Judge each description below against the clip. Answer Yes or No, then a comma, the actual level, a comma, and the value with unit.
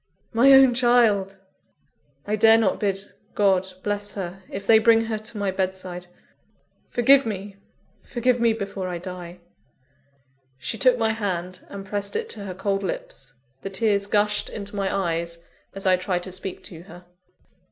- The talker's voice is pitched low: No, high, 200 Hz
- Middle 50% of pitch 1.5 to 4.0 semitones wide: Yes, average, 3.0 semitones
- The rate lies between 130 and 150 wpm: No, average, 165 wpm